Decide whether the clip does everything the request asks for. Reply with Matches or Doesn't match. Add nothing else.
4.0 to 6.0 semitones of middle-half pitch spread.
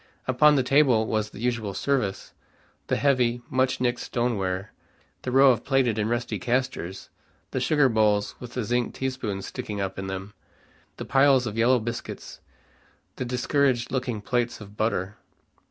Doesn't match